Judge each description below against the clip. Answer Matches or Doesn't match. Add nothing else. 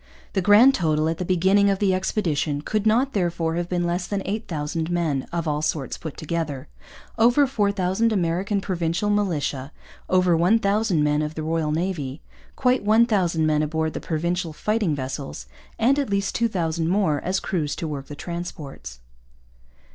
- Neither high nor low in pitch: Matches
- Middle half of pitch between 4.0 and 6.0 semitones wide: Matches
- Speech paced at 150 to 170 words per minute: Matches